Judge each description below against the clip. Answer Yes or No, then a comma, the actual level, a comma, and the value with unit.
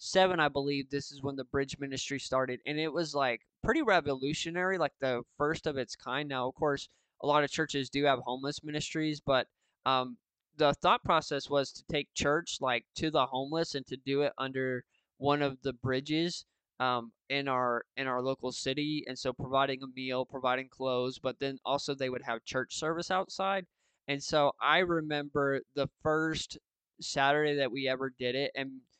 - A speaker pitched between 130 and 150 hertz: Yes, medium, 140 Hz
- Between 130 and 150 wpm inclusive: No, average, 190 wpm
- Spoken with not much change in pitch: Yes, narrow, 2.3 semitones